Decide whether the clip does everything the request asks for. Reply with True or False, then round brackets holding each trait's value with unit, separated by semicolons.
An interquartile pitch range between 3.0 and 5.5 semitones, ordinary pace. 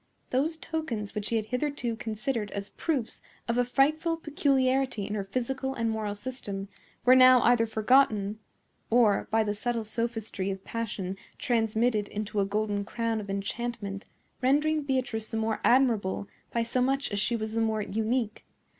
True (3.4 semitones; 165 wpm)